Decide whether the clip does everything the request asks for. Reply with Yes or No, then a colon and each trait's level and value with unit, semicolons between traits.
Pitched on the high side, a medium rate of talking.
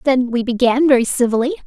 Yes: very high, 250 Hz; average, 145 wpm